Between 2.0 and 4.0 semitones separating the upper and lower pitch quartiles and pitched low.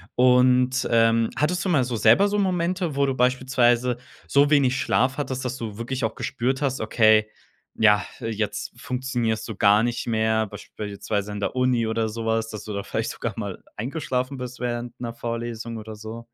Yes: average, 2.7 semitones; low, 120 Hz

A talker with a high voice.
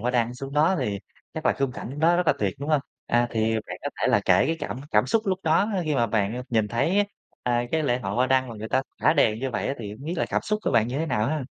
No: low, 130 Hz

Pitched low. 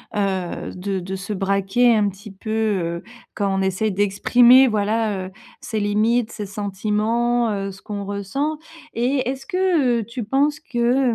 No: high, 210 Hz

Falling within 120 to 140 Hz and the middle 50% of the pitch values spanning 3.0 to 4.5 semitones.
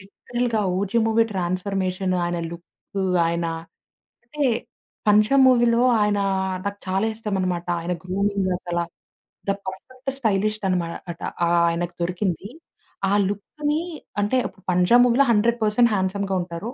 No: high, 200 Hz; average, 3.7 semitones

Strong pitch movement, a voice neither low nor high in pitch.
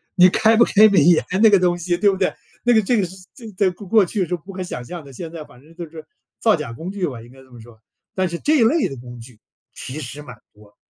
Yes: wide, 6.7 semitones; medium, 175 Hz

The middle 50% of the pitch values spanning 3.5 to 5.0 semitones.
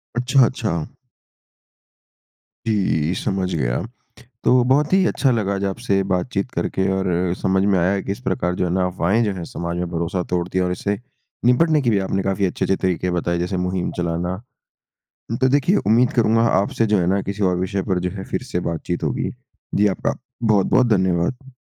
Yes: average, 4.1 semitones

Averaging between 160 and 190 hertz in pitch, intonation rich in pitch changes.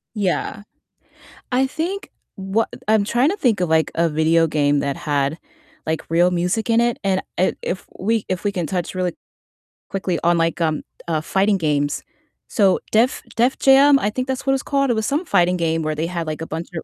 Yes: medium, 185 Hz; wide, 5.9 semitones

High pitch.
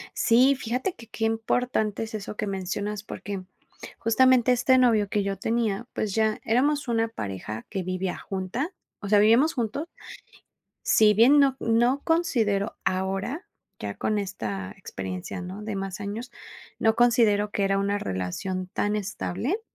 Yes: high, 215 Hz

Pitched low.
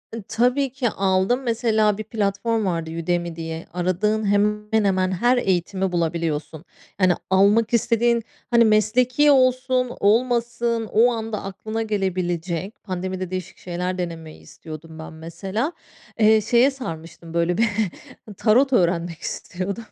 No: high, 205 Hz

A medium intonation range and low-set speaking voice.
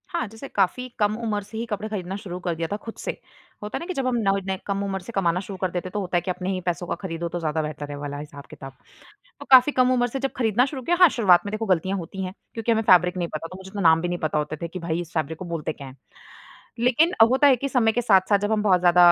No: average, 4.6 semitones; high, 190 Hz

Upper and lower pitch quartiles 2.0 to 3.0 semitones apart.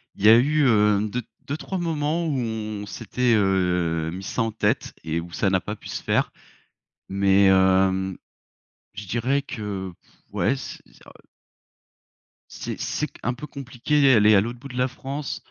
No: wide, 5.4 semitones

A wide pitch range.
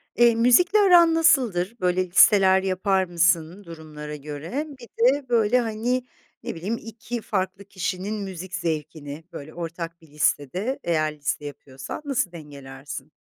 Yes: wide, 6.5 semitones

